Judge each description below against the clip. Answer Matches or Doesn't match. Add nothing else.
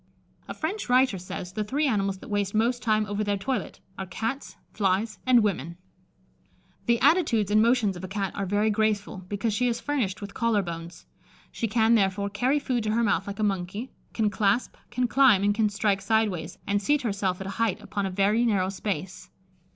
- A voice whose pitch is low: Doesn't match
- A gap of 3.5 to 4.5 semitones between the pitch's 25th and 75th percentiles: Doesn't match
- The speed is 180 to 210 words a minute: Matches